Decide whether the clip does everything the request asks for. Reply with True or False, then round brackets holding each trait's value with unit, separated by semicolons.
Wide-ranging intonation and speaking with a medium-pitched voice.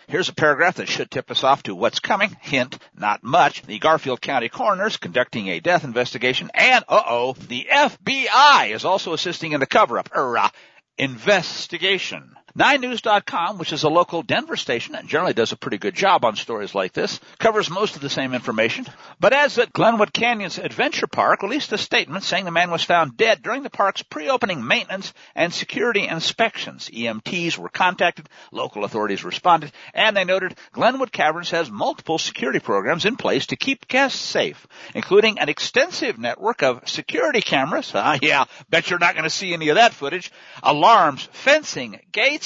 True (6.2 semitones; 175 Hz)